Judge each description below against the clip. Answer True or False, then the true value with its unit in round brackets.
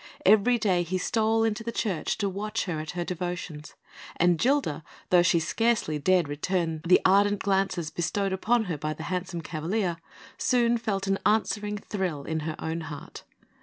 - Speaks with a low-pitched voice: False (185 Hz)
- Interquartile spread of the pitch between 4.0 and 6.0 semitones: True (4.3 semitones)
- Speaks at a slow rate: False (170 wpm)